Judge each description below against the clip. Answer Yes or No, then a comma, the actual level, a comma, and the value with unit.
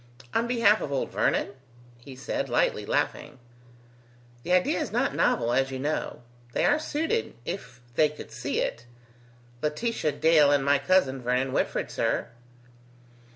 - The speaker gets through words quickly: No, average, 150 wpm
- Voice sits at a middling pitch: Yes, medium, 145 Hz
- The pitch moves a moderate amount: No, wide, 6.0 semitones